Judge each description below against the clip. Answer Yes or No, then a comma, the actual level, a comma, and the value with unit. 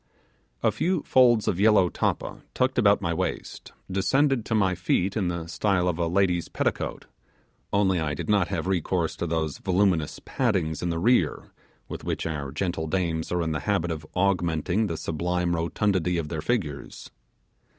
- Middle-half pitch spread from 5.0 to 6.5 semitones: No, average, 3.5 semitones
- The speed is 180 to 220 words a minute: No, average, 170 wpm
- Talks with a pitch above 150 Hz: No, very low, 90 Hz